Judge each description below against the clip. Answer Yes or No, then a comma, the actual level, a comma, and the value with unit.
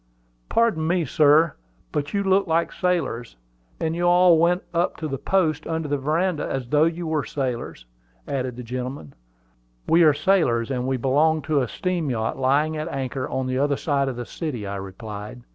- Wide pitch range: No, average, 4.5 semitones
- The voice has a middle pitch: Yes, medium, 145 Hz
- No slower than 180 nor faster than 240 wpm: Yes, average, 185 wpm